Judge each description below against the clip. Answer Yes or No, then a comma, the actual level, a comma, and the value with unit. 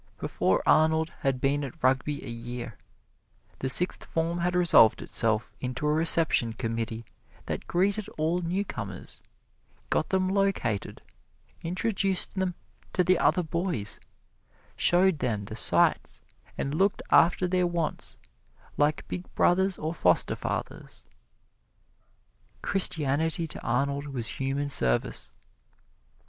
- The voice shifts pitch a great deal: Yes, wide, 6.0 semitones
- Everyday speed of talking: No, slow, 120 wpm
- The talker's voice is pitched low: No, medium, 155 Hz